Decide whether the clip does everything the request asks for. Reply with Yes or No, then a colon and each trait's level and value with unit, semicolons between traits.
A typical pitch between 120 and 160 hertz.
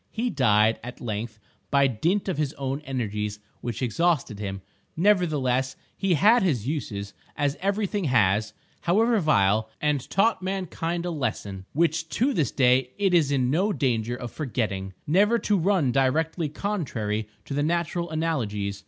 Yes: medium, 140 Hz